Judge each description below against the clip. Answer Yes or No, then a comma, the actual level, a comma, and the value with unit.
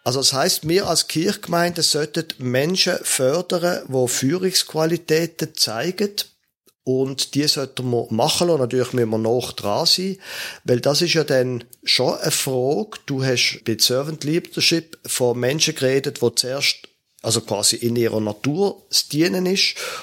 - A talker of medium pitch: Yes, medium, 145 Hz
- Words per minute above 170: No, average, 150 wpm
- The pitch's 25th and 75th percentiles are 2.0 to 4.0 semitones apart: No, average, 5.2 semitones